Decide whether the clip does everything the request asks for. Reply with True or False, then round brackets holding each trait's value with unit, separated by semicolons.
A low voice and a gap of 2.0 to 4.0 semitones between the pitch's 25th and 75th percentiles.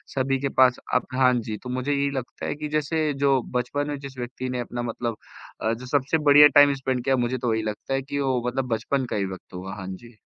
True (130 Hz; 2.7 semitones)